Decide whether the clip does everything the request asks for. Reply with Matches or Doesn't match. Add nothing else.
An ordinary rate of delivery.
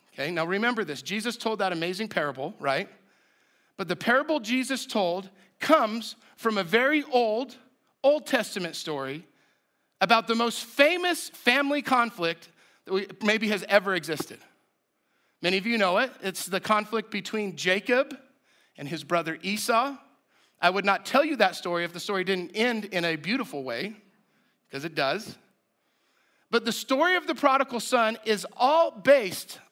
Matches